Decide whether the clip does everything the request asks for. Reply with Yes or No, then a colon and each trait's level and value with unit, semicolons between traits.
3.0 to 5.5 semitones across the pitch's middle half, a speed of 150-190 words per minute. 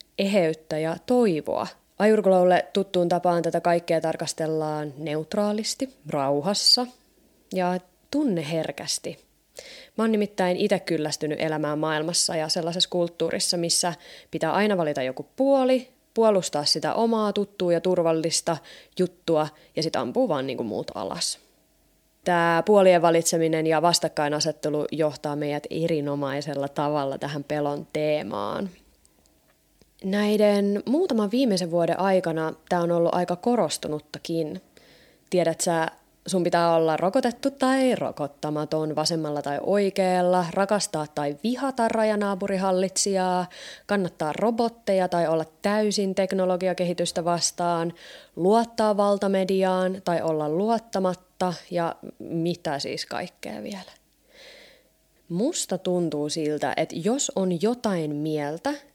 No: average, 4.3 semitones; average, 105 wpm